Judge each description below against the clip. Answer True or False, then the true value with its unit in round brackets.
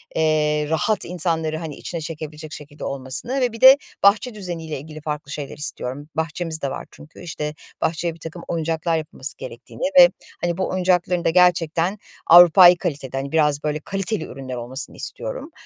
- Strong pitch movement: False (3.0 semitones)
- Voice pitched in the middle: True (160 Hz)